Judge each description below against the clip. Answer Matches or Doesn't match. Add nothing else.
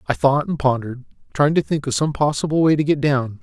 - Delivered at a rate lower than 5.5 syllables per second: Doesn't match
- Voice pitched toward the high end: Doesn't match